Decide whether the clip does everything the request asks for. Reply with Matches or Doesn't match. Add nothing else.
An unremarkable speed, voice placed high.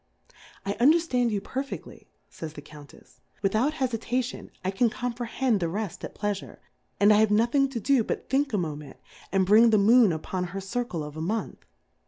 Matches